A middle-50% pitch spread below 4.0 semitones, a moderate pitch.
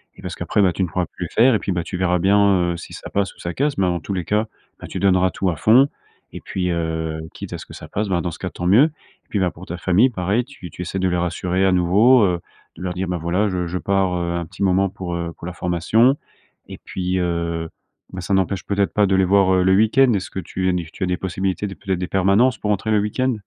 No: narrow, 2.4 semitones; very low, 95 Hz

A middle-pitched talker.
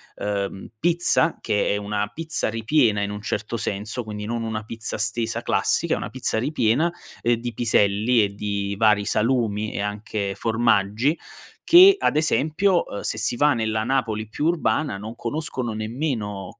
No: low, 110 Hz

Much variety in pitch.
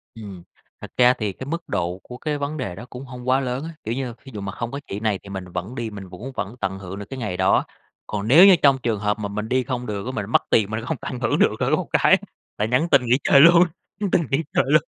No: average, 4.7 semitones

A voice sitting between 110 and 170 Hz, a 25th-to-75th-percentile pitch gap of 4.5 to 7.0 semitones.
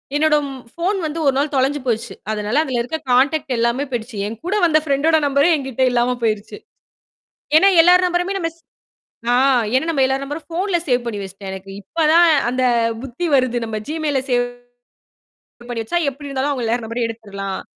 No: very high, 265 Hz; average, 5.2 semitones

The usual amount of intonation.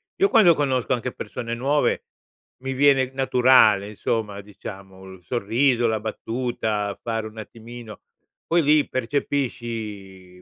Yes: average, 3.9 semitones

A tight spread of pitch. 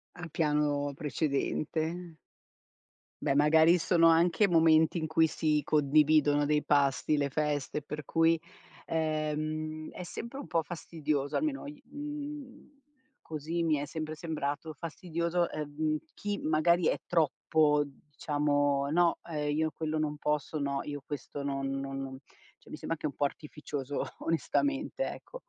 Yes: narrow, 2.3 semitones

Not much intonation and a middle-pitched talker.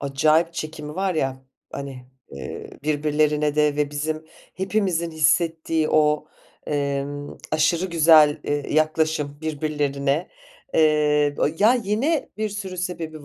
Yes: narrow, 2.2 semitones; medium, 155 Hz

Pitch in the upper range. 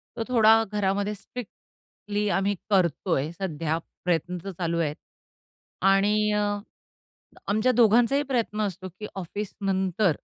Yes: high, 200 Hz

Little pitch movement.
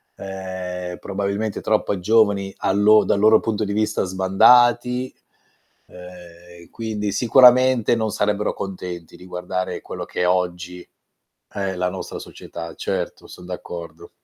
No: average, 3.1 semitones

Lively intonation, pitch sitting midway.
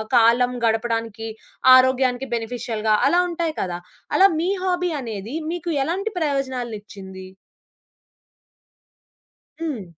No: wide, 5.9 semitones; high, 245 Hz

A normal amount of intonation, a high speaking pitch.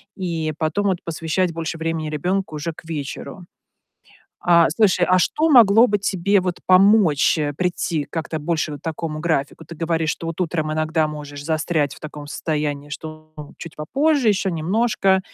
No: average, 3.2 semitones; medium, 165 Hz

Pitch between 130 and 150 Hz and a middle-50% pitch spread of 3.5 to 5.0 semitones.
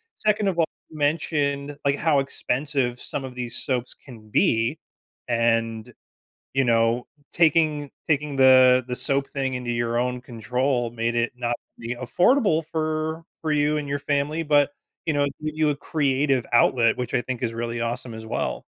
Yes: low, 135 Hz; average, 3.8 semitones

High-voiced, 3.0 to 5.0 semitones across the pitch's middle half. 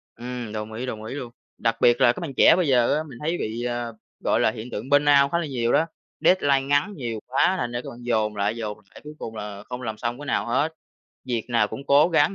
No: low, 120 Hz; average, 3.9 semitones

